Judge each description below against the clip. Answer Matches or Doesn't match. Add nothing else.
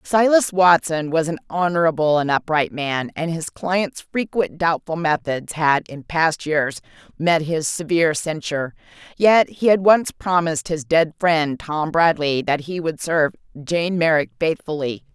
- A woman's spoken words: Matches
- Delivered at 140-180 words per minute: Matches